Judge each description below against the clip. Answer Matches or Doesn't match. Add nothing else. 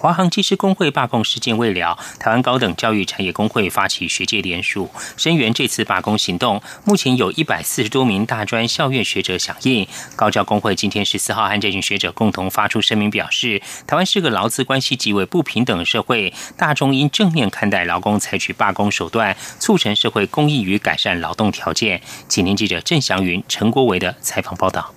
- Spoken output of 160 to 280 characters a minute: Doesn't match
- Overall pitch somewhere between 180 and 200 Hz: Doesn't match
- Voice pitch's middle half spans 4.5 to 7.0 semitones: Matches